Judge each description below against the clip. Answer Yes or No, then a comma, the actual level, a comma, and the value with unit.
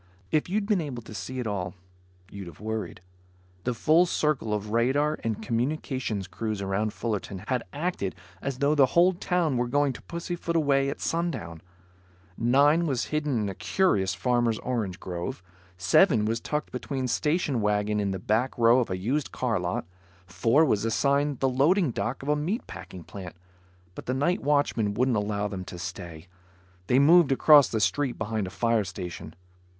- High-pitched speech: No, low, 120 Hz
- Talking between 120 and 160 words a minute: No, average, 175 wpm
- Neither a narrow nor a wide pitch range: No, wide, 6.0 semitones